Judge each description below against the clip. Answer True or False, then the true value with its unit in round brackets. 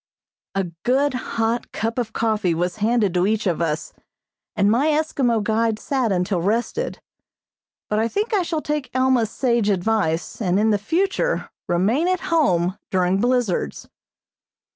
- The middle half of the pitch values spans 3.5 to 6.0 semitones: True (5.0 semitones)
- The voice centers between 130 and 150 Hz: False (225 Hz)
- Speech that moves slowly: False (145 wpm)